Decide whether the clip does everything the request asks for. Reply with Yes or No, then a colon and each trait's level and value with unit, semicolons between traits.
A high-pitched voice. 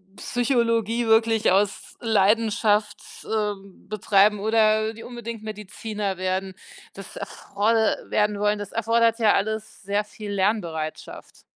Yes: high, 215 Hz